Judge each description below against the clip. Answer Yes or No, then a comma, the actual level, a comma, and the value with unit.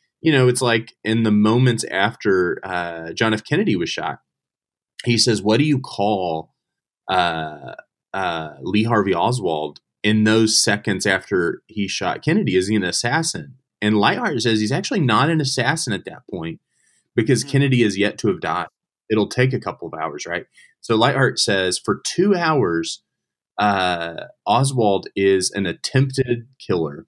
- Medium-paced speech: Yes, average, 160 wpm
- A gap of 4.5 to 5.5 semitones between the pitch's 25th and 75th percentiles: Yes, average, 4.9 semitones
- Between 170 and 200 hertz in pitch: No, low, 110 Hz